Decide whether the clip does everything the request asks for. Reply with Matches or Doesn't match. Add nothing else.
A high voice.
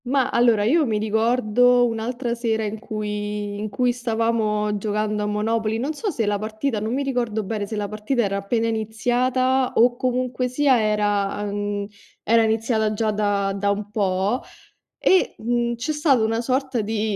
Matches